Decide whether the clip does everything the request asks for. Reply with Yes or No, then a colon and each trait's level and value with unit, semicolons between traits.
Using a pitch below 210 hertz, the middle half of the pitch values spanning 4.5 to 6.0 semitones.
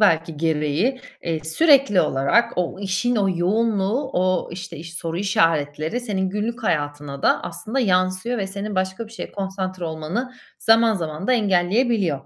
Yes: high, 190 Hz; average, 5.3 semitones